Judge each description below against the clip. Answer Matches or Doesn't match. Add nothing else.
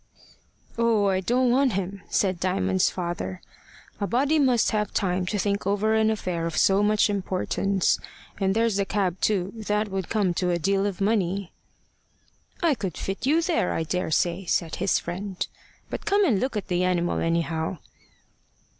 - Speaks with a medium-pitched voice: Doesn't match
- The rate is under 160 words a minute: Doesn't match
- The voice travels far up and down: Doesn't match